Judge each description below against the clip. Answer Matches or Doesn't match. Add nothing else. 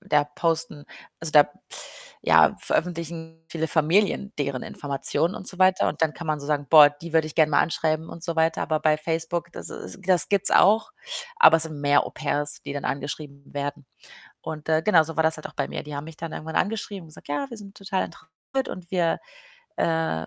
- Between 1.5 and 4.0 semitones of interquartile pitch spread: Matches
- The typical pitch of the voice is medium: Matches